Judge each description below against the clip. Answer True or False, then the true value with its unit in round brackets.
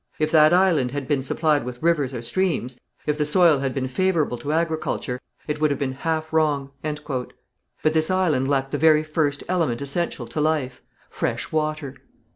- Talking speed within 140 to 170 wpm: False (180 wpm)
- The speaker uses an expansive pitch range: False (2.8 semitones)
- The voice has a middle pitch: True (150 Hz)